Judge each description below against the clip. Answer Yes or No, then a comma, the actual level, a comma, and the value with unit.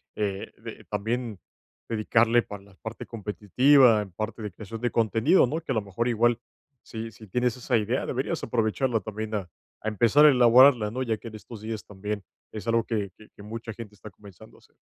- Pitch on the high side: No, low, 110 Hz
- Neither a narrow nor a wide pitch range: No, narrow, 2.3 semitones